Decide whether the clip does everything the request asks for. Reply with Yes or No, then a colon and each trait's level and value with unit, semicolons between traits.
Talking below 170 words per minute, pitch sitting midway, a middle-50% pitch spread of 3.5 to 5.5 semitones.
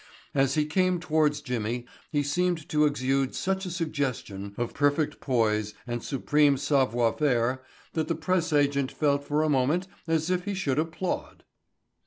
Yes: average, 160 wpm; medium, 145 Hz; average, 3.8 semitones